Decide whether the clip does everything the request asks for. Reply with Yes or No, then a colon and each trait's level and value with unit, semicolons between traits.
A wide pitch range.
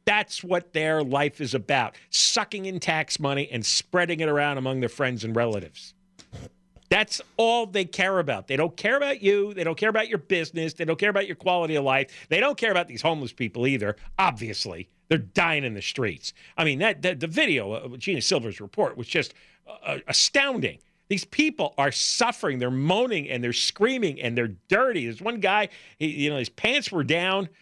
Yes: wide, 6.9 semitones